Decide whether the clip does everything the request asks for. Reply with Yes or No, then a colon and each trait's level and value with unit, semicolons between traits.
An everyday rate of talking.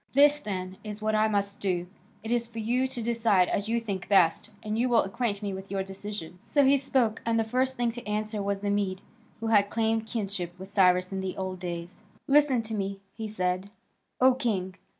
No: fast, 215 wpm